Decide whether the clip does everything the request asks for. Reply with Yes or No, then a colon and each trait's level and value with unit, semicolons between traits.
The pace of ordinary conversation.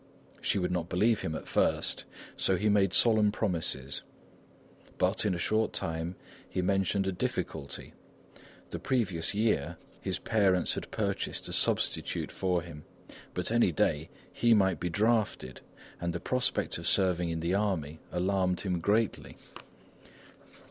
Yes: average, 145 wpm